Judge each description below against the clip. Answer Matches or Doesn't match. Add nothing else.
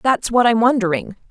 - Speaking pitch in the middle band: Doesn't match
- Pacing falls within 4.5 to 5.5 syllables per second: Matches